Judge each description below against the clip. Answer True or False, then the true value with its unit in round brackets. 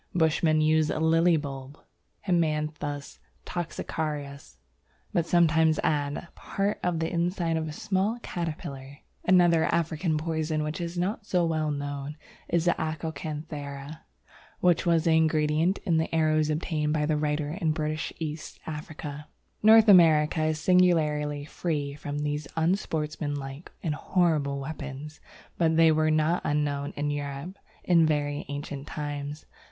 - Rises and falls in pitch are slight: True (2.2 semitones)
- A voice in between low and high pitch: True (155 Hz)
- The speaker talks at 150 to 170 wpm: False (135 wpm)